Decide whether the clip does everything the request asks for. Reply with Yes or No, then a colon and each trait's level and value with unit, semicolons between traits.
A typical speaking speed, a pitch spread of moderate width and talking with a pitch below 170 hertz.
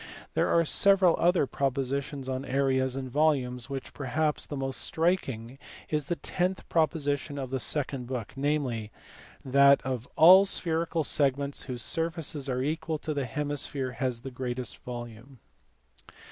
Yes: average, 145 wpm; average, 3.2 semitones; medium, 140 Hz